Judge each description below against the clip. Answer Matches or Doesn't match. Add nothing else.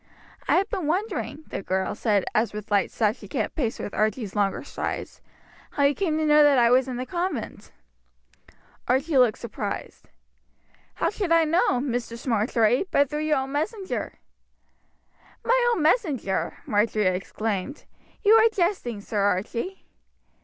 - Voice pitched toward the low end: Doesn't match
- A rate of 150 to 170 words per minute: Matches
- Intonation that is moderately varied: Doesn't match